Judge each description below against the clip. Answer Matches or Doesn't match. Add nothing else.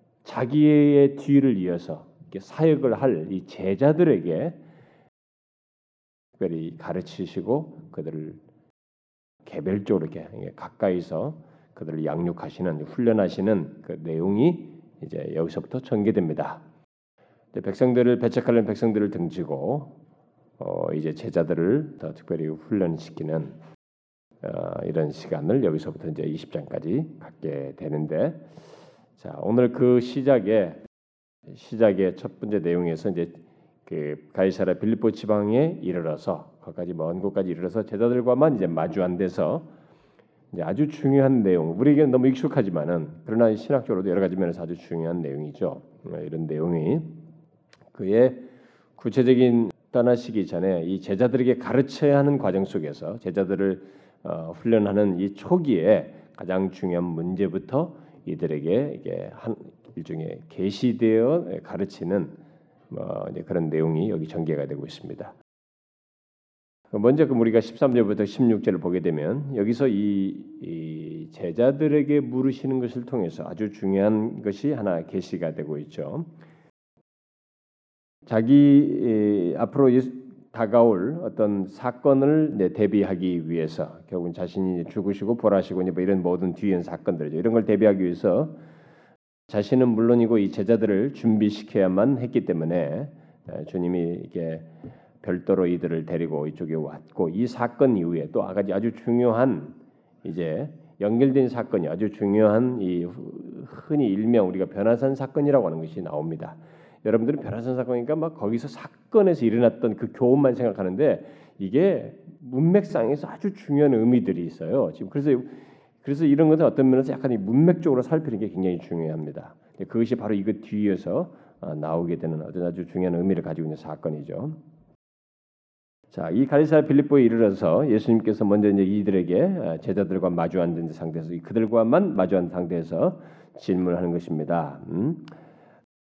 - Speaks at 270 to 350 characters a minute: Matches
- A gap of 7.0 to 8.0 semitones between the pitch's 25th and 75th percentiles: Doesn't match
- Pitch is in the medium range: Doesn't match